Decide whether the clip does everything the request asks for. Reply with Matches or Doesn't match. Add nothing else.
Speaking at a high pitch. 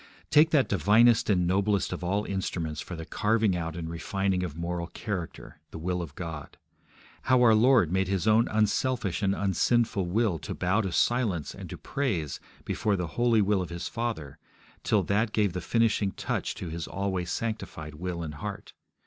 Doesn't match